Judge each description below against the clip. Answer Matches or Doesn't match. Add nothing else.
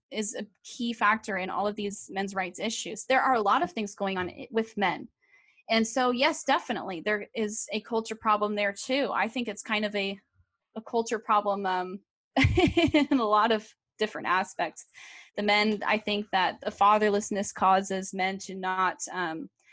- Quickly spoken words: Doesn't match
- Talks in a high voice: Matches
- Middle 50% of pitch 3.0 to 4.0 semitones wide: Doesn't match